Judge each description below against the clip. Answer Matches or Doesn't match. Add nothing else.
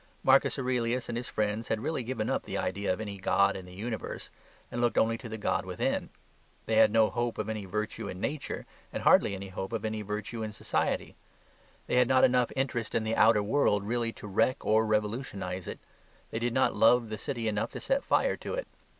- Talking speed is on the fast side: Matches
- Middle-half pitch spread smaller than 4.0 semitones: Matches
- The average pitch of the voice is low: Matches